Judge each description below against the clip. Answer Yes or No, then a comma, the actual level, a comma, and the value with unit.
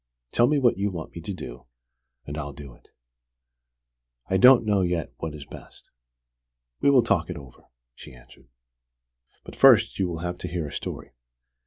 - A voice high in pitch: No, very low, 85 Hz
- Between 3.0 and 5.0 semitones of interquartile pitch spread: No, wide, 5.6 semitones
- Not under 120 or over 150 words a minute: No, average, 180 wpm